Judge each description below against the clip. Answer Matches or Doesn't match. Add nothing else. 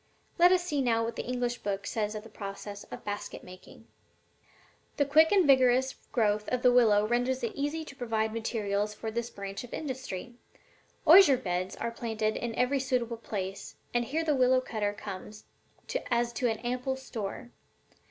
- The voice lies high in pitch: Matches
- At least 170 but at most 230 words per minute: Matches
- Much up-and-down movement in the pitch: Doesn't match